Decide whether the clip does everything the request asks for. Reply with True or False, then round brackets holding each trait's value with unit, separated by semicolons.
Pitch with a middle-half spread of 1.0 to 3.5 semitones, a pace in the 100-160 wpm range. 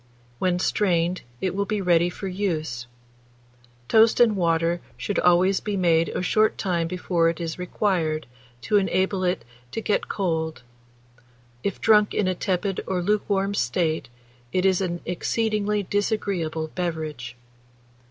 True (3.2 semitones; 140 wpm)